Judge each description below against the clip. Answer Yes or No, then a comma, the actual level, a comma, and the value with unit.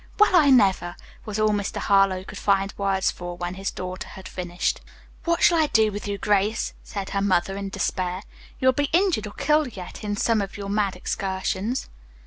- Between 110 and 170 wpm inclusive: No, average, 200 wpm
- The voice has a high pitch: Yes, high, 200 Hz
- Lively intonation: No, narrow, 2.6 semitones